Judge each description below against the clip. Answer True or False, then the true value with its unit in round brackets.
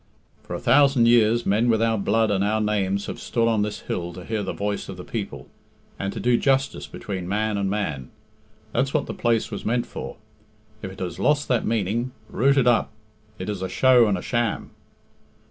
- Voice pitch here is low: True (110 Hz)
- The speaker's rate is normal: False (210 wpm)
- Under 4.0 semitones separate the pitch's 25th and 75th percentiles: True (3.3 semitones)